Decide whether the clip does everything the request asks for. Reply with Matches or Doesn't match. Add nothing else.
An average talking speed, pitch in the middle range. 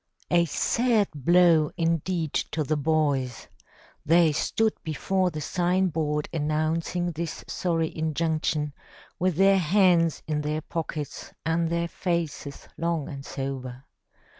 Doesn't match